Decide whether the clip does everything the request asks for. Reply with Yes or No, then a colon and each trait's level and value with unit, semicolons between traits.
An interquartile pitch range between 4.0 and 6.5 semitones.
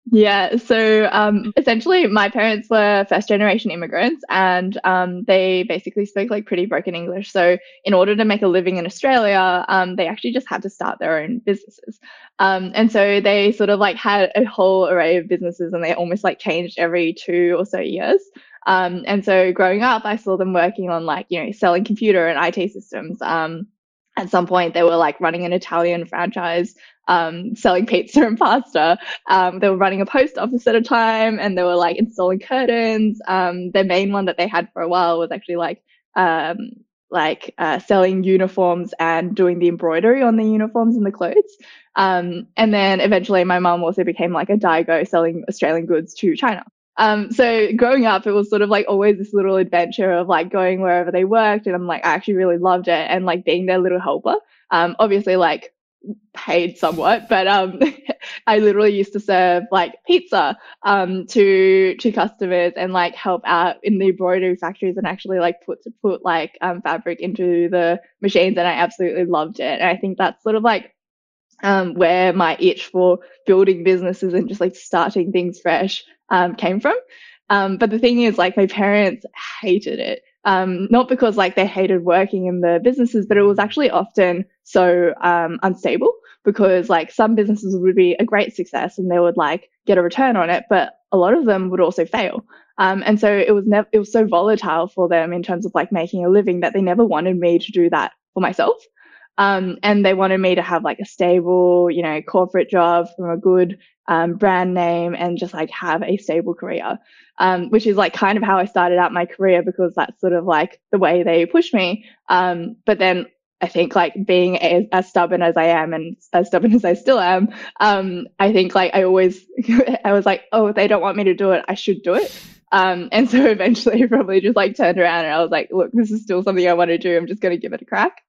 No: average, 3.0 semitones